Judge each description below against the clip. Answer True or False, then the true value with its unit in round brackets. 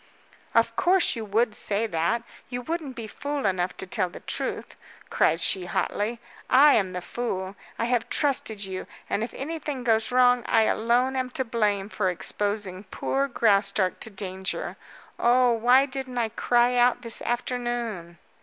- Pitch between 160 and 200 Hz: False (230 Hz)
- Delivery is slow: False (165 wpm)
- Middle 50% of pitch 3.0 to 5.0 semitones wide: True (3.9 semitones)